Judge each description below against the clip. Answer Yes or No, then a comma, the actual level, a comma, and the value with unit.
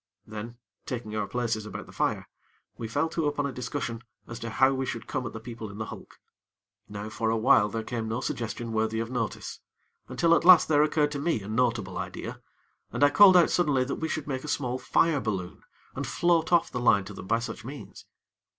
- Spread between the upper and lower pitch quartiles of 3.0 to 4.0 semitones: No, average, 4.6 semitones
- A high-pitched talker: No, low, 120 Hz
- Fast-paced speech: Yes, fast, 225 wpm